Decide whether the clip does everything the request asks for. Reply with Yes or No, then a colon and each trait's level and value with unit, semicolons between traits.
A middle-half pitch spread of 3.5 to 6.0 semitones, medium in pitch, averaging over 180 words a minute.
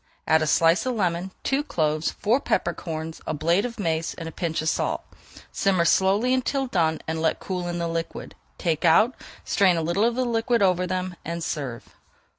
Yes: average, 4.0 semitones; medium, 175 Hz; average, 200 wpm